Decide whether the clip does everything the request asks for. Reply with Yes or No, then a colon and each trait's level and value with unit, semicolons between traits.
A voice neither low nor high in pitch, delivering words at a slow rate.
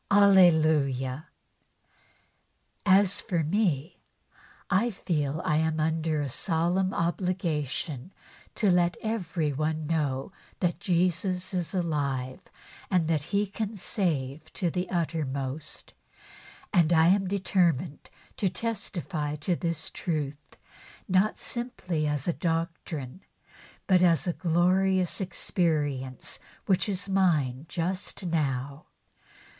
Yes: medium, 170 Hz; slow, 105 wpm